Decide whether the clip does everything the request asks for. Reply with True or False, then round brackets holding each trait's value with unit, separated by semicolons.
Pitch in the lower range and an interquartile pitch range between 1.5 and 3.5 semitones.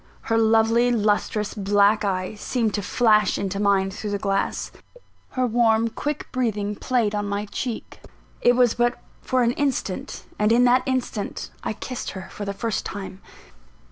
False (215 Hz; 3.0 semitones)